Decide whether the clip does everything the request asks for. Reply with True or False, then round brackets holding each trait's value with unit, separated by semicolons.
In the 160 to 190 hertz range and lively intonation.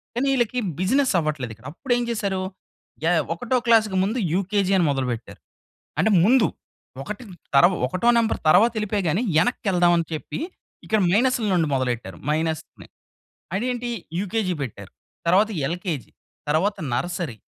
True (185 Hz; 6.1 semitones)